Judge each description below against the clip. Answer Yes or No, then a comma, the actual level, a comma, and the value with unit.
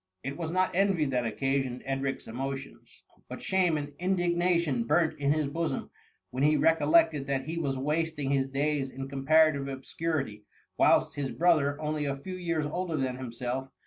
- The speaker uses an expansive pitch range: No, average, 3.4 semitones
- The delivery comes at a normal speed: Yes, average, 170 wpm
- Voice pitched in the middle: Yes, medium, 145 Hz